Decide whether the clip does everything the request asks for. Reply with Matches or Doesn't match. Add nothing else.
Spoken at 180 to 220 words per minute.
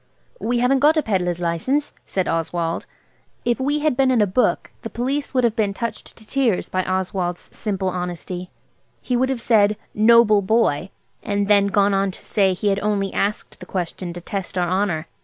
Matches